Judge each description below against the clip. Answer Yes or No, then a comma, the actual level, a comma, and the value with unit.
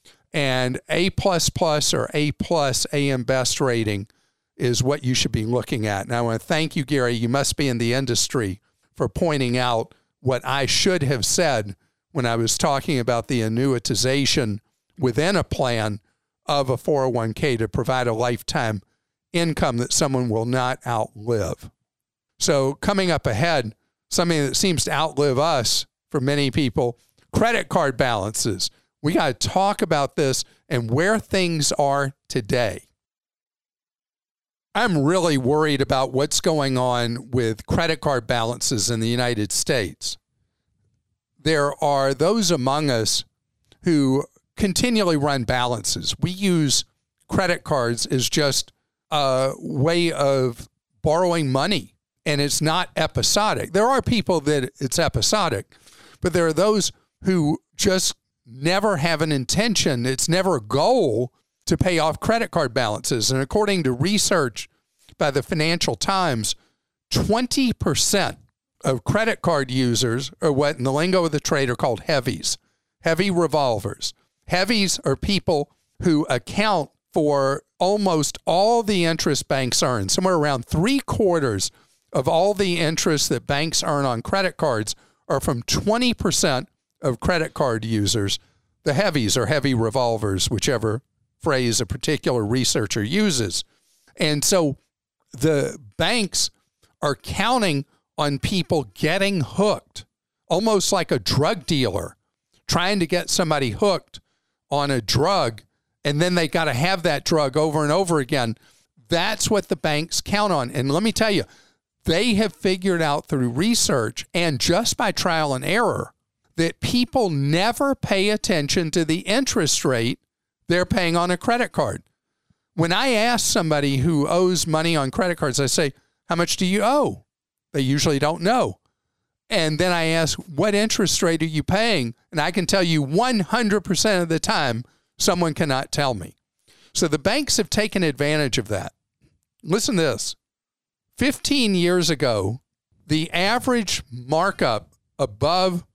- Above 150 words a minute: No, average, 145 wpm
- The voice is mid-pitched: Yes, medium, 150 Hz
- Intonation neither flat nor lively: No, wide, 6.1 semitones